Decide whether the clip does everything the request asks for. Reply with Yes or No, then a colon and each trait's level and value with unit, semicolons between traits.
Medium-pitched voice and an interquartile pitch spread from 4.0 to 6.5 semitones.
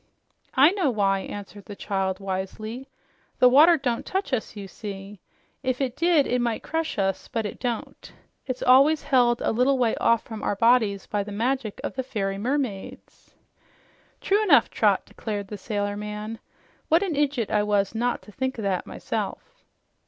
No: high, 230 Hz; average, 4.6 semitones